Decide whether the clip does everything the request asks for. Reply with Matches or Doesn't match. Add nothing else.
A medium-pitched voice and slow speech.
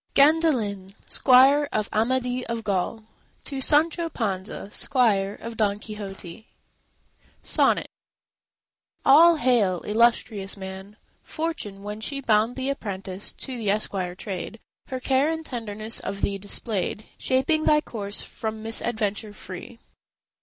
Doesn't match